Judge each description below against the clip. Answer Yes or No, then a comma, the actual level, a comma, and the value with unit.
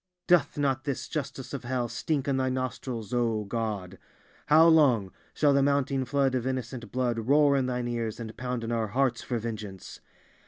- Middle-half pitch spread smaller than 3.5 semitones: Yes, average, 3.0 semitones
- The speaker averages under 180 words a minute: No, average, 185 wpm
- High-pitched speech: No, low, 125 Hz